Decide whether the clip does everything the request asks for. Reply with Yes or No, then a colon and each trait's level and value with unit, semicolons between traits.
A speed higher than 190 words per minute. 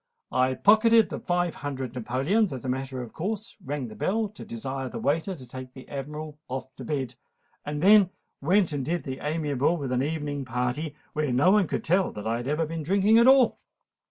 Yes: average, 200 wpm